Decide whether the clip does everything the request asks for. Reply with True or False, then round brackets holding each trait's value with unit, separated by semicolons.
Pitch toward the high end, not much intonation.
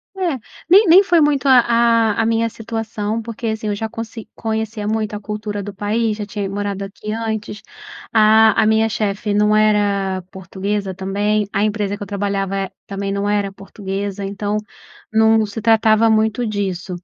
True (210 Hz; 1.7 semitones)